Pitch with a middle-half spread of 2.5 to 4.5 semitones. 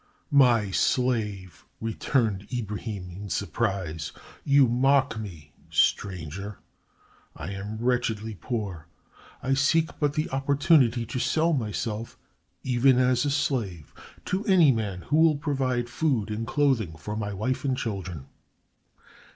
No: average, 5.1 semitones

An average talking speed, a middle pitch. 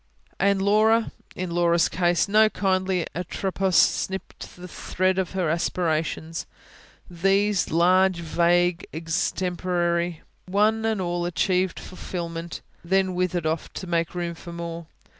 No: slow, 120 wpm; medium, 180 Hz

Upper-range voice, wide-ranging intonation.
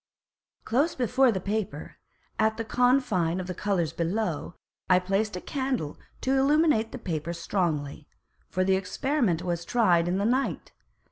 Yes: high, 195 Hz; wide, 6.2 semitones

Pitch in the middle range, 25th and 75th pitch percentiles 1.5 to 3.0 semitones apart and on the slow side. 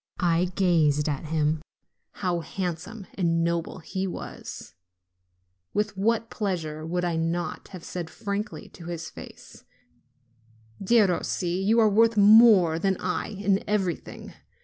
No: medium, 180 Hz; average, 3.7 semitones; slow, 125 wpm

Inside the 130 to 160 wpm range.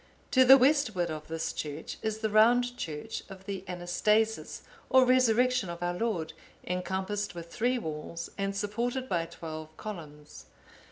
Yes: average, 150 wpm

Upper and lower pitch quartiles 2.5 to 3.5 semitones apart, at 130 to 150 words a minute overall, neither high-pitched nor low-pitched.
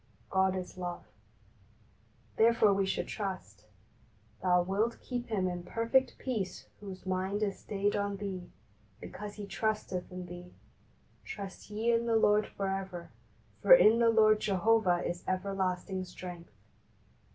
No: average, 2.8 semitones; average, 140 wpm; high, 195 Hz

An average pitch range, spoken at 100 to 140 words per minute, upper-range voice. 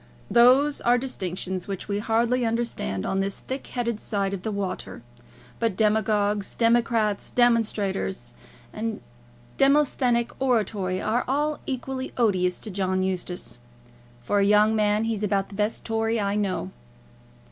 Yes: average, 3.3 semitones; slow, 135 wpm; high, 215 Hz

